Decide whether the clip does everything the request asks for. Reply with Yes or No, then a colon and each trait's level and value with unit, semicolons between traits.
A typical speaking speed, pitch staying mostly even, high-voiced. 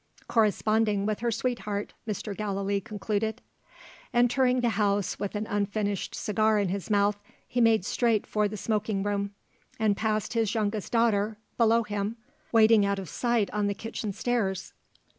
Yes: average, 155 wpm; narrow, 1.9 semitones; high, 210 Hz